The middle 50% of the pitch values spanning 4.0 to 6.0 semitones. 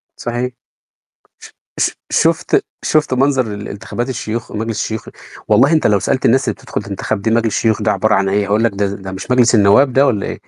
No: average, 3.6 semitones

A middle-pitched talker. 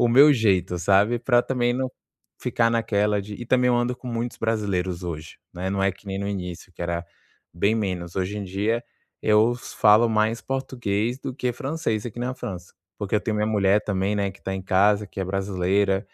No: low, 105 Hz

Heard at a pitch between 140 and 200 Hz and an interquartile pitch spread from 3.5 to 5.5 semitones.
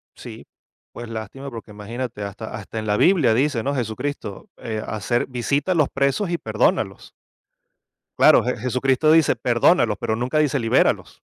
No: low, 125 Hz; average, 4.2 semitones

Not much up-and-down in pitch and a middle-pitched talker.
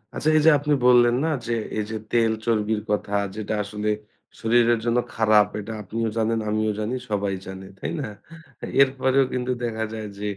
No: narrow, 2.2 semitones; low, 110 Hz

